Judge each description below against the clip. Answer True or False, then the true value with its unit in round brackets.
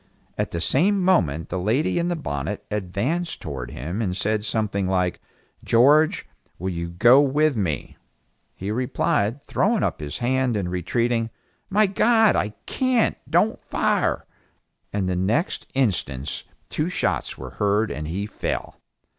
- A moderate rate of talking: True (145 wpm)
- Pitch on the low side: True (105 Hz)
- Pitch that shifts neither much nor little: False (8.3 semitones)